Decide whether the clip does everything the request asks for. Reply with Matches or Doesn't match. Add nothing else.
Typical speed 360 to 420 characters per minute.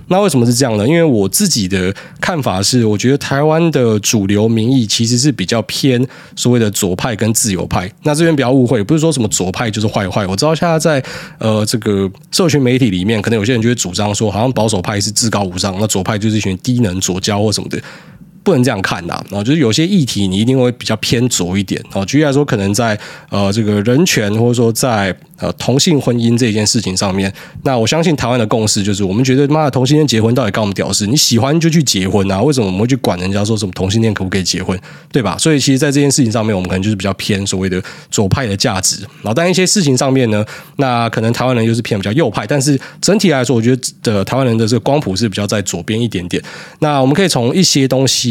Matches